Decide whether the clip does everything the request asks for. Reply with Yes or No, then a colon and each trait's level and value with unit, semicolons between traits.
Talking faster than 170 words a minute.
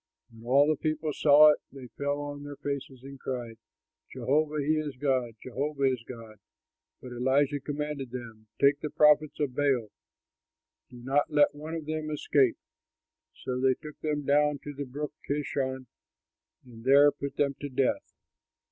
No: average, 165 wpm